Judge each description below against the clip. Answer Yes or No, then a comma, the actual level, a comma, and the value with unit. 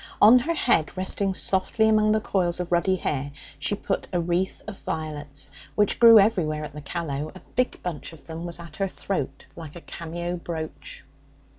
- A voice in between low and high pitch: Yes, medium, 175 Hz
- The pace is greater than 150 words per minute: Yes, average, 185 wpm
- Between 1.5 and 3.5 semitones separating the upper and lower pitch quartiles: No, average, 4.1 semitones